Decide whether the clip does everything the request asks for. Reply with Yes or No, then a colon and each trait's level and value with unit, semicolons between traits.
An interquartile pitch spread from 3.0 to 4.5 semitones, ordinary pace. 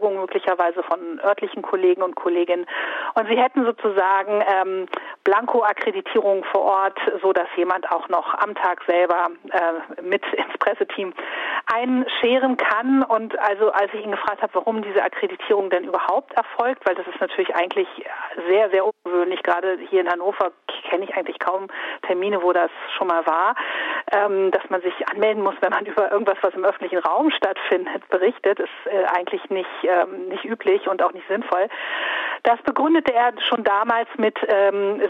Yes: average, 3.7 semitones; average, 165 wpm